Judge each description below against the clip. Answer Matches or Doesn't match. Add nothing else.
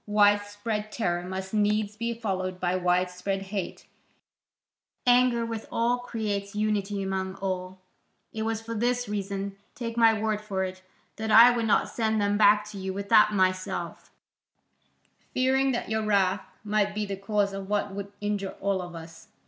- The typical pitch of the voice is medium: Doesn't match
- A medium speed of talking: Matches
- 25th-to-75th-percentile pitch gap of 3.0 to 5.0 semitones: Doesn't match